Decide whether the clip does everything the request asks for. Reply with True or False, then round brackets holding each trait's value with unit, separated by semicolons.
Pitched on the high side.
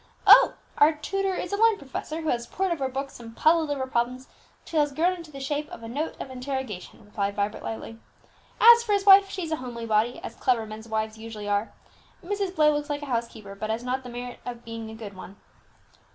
True (260 Hz)